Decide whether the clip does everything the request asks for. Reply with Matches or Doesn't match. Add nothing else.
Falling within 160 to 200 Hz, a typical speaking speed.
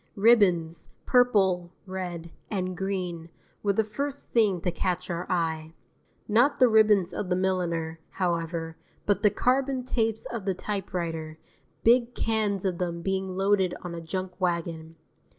Matches